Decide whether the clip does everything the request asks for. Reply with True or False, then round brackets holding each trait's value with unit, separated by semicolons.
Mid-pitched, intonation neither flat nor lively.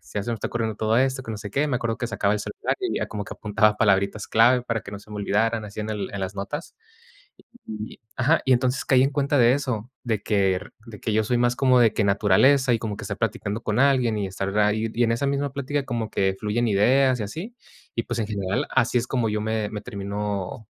False (110 Hz; 3.4 semitones)